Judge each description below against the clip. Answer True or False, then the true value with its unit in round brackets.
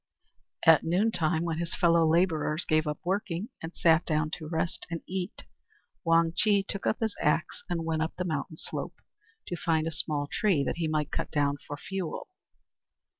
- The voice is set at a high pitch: False (165 Hz)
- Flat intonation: True (2.1 semitones)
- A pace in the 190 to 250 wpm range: False (175 wpm)